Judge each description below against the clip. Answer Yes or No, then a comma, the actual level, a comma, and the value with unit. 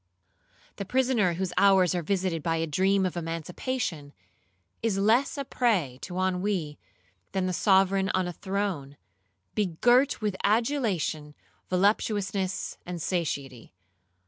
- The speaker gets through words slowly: Yes, slow, 120 wpm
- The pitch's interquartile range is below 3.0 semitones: No, average, 3.6 semitones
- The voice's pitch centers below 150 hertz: No, high, 190 Hz